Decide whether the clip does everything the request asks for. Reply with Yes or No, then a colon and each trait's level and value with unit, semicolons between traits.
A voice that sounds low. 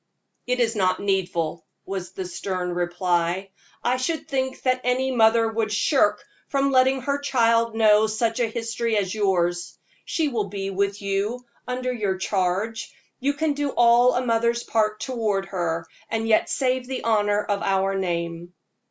No: high, 220 Hz